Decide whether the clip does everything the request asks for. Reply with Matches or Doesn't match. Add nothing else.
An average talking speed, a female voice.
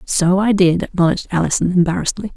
Matches